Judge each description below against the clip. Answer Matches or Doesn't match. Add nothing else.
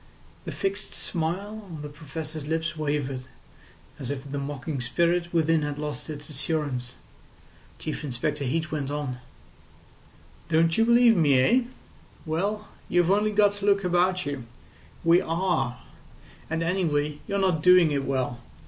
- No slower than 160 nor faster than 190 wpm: Doesn't match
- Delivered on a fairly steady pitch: Doesn't match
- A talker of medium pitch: Matches